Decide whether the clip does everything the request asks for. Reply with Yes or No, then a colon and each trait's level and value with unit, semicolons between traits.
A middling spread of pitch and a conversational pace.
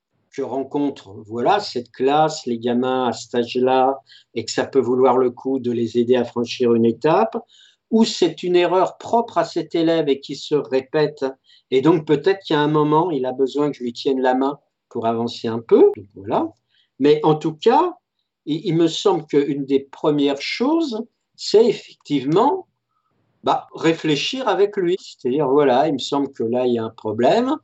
No: wide, 7.3 semitones; average, 195 wpm